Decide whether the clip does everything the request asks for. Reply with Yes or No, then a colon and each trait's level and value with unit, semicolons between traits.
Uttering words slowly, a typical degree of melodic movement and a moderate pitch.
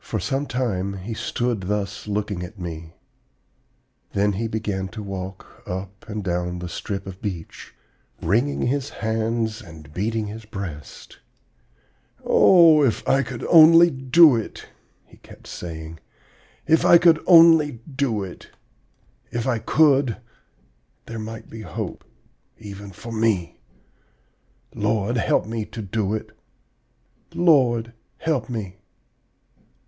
No: slow, 125 wpm; average, 4.4 semitones; low, 110 Hz